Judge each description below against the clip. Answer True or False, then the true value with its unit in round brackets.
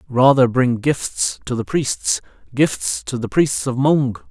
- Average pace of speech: True (165 wpm)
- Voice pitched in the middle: False (125 Hz)